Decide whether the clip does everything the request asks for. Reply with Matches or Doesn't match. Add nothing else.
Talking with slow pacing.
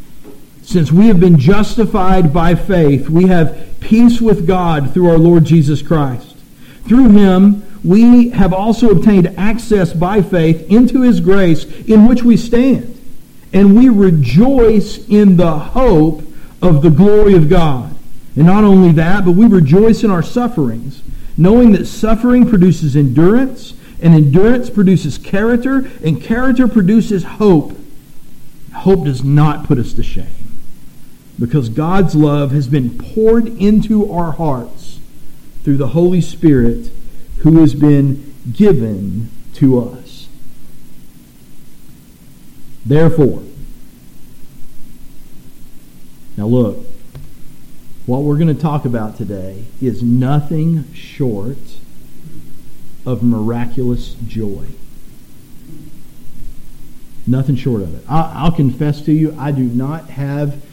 Matches